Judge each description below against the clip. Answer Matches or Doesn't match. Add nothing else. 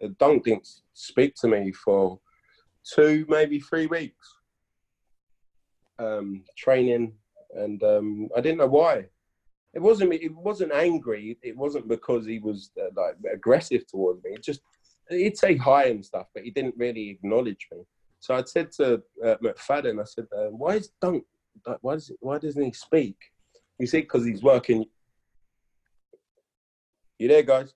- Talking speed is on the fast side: Doesn't match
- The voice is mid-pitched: Matches